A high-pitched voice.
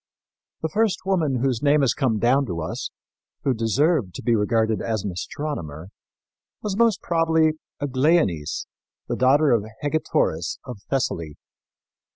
No: low, 130 Hz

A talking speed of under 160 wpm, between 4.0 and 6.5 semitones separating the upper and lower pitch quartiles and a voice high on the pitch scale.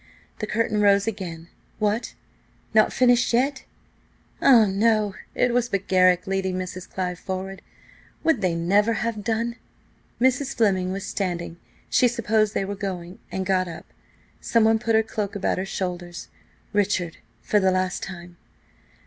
No: average, 140 wpm; average, 3.4 semitones; high, 200 Hz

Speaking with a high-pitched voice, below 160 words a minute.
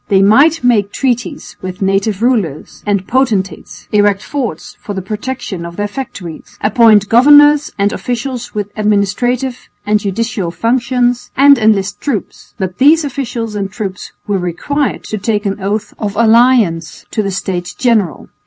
Yes: high, 215 Hz; average, 150 wpm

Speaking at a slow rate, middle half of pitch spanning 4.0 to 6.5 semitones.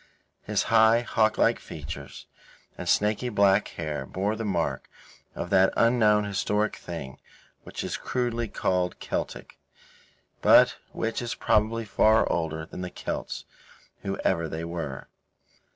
Yes: slow, 125 wpm; average, 4.8 semitones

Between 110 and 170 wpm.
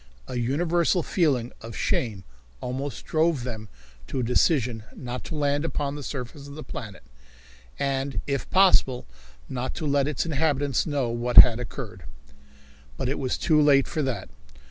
Yes: average, 160 wpm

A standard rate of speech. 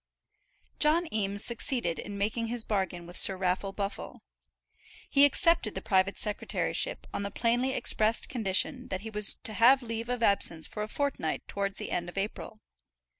Yes: average, 170 wpm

